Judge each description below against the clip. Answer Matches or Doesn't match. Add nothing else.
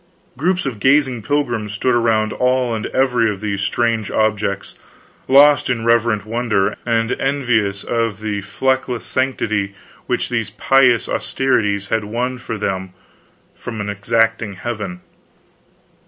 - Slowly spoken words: Matches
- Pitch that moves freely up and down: Doesn't match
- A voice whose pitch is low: Matches